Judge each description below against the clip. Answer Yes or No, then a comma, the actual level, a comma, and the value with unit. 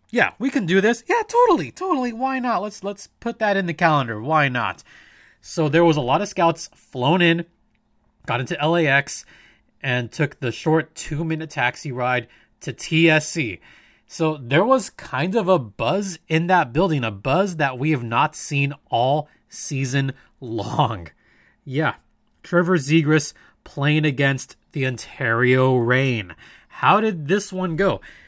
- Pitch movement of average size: No, wide, 5.9 semitones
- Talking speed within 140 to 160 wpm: Yes, average, 155 wpm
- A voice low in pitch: No, medium, 155 Hz